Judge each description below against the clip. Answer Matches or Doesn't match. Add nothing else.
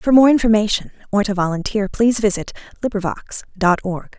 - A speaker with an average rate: Matches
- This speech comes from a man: Doesn't match